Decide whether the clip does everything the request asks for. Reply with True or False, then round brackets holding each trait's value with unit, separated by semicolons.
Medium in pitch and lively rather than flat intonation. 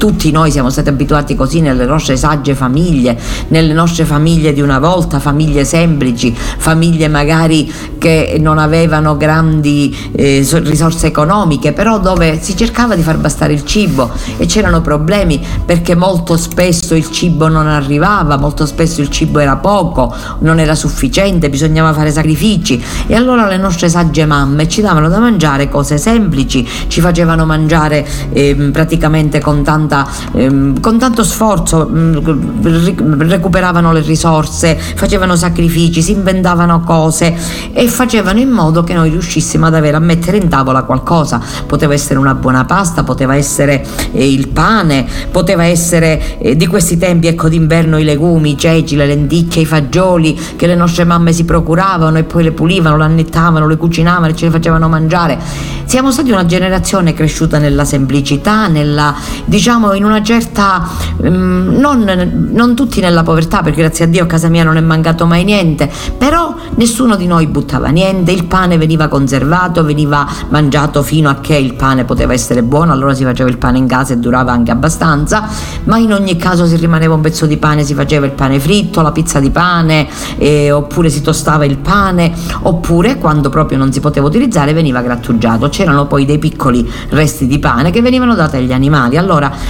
False (160 Hz; 3.2 semitones)